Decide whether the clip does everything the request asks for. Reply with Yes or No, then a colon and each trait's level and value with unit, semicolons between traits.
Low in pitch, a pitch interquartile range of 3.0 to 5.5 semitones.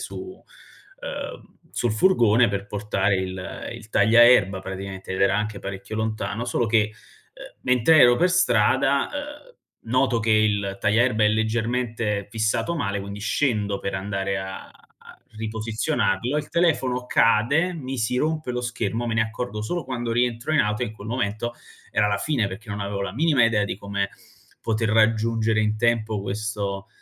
Yes: low, 110 Hz; average, 3.3 semitones